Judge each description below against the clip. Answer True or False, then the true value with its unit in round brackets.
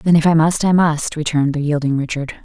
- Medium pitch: True (155 Hz)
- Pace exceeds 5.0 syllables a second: True (5.9 syllables/s)